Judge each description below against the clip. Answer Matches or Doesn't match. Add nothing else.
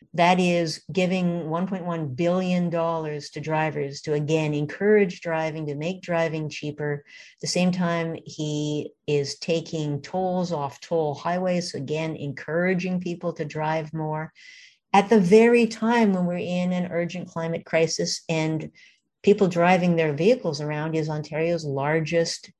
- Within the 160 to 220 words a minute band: Doesn't match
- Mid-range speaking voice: Matches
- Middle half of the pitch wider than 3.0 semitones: Doesn't match